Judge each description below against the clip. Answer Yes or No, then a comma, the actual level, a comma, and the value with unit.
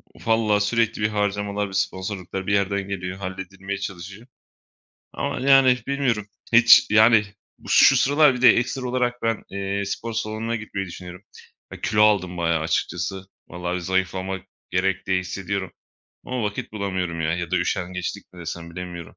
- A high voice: No, low, 100 Hz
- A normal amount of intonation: Yes, average, 3.1 semitones